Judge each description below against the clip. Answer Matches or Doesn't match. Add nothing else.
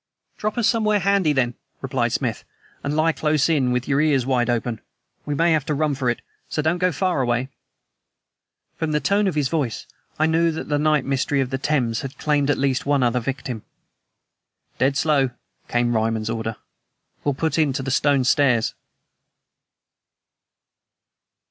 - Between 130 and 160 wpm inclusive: Doesn't match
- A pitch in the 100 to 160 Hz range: Matches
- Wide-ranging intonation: Doesn't match